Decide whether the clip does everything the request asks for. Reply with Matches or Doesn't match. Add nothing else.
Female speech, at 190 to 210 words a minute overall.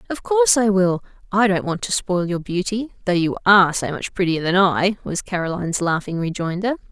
Matches